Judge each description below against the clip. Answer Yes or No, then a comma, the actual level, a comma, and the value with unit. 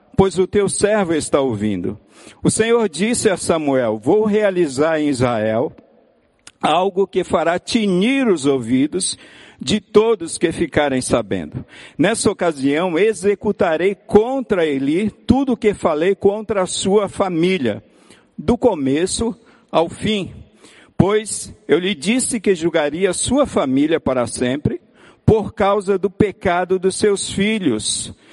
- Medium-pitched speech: No, high, 195 Hz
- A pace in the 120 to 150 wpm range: Yes, average, 125 wpm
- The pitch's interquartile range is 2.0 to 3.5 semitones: No, average, 4.8 semitones